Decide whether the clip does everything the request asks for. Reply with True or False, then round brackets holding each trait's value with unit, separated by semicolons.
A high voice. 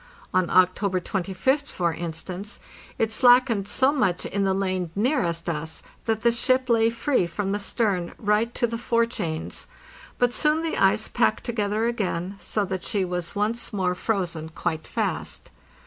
True (205 Hz)